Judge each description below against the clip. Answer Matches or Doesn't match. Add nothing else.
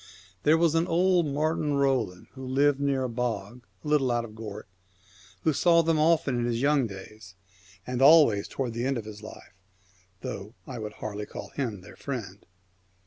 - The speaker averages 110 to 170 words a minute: Doesn't match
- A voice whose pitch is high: Doesn't match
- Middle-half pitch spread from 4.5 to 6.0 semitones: Matches